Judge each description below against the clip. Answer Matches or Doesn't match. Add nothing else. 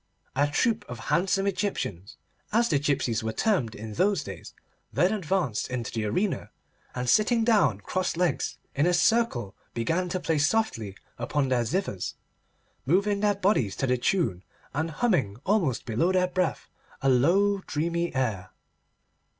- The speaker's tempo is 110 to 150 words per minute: Matches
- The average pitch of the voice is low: Doesn't match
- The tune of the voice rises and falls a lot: Matches